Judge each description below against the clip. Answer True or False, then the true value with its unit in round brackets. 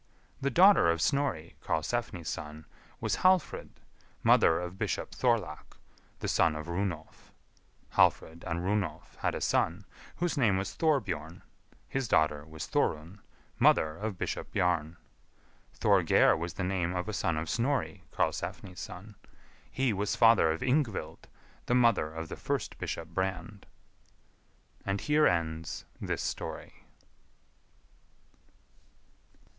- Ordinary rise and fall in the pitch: False (5.9 semitones)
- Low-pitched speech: True (90 Hz)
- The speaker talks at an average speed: False (125 wpm)